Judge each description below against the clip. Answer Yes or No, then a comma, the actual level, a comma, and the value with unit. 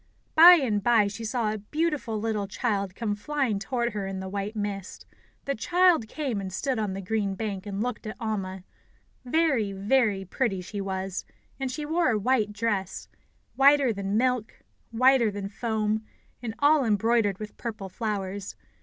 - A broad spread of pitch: No, average, 4.1 semitones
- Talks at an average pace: Yes, average, 170 wpm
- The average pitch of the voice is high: Yes, high, 215 Hz